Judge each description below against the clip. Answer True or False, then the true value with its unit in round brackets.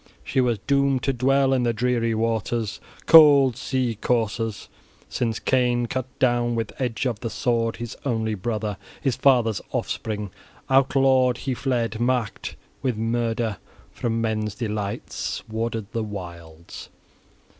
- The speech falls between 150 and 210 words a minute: False (135 wpm)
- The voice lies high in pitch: False (115 Hz)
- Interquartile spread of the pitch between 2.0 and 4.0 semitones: True (2.5 semitones)